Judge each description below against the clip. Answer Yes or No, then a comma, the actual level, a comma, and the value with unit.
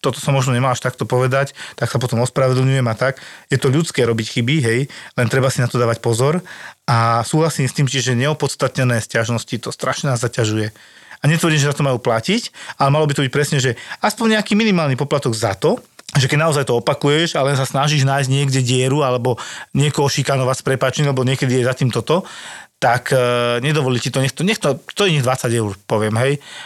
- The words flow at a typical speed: No, fast, 215 wpm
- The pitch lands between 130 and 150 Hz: Yes, low, 135 Hz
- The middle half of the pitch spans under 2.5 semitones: No, average, 2.8 semitones